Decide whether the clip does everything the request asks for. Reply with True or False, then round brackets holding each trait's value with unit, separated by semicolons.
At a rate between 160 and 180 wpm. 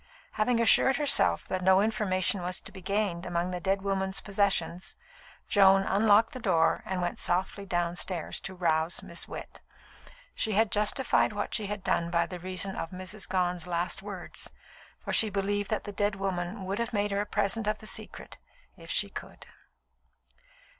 True (170 wpm)